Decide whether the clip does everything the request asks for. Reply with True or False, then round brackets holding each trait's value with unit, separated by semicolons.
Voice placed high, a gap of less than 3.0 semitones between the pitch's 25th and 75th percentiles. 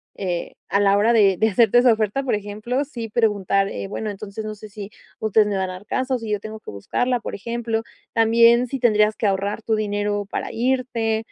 True (215 Hz; 2.4 semitones)